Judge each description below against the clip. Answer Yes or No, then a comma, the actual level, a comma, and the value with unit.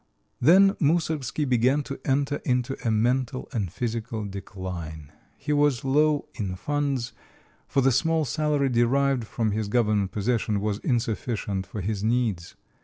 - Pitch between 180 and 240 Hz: No, low, 120 Hz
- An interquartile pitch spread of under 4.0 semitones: No, average, 4.8 semitones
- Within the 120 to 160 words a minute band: Yes, average, 140 wpm